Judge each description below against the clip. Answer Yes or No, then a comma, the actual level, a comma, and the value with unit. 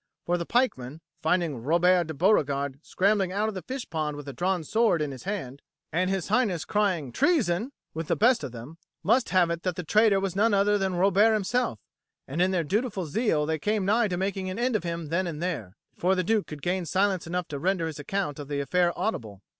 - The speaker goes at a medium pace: No, fast, 225 wpm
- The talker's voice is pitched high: No, medium, 180 Hz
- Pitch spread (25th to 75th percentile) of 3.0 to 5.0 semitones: Yes, average, 4.5 semitones